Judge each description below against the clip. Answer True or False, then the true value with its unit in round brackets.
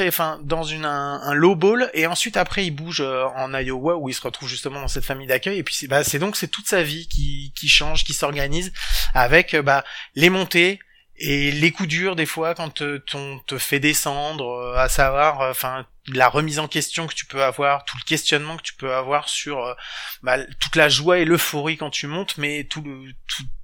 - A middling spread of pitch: True (3.1 semitones)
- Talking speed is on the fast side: True (230 wpm)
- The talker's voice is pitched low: False (145 Hz)